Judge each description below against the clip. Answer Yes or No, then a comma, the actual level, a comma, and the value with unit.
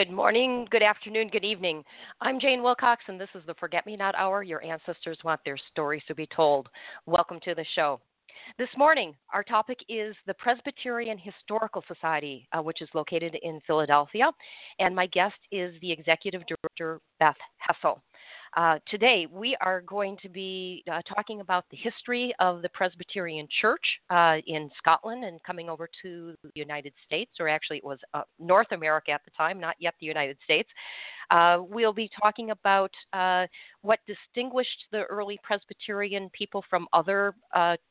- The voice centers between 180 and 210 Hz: Yes, medium, 185 Hz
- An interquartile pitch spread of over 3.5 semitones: Yes, average, 4.5 semitones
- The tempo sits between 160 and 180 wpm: Yes, average, 175 wpm